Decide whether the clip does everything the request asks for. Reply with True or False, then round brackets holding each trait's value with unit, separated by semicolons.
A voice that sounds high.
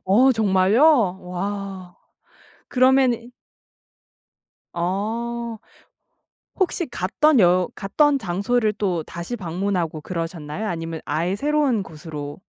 True (195 Hz)